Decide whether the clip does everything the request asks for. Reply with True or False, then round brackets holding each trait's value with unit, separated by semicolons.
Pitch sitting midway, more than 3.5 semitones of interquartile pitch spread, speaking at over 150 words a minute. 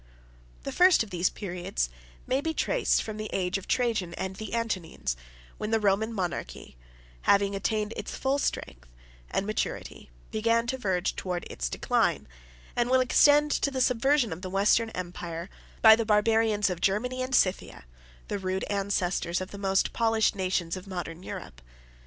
False (200 Hz; 3.9 semitones; 165 wpm)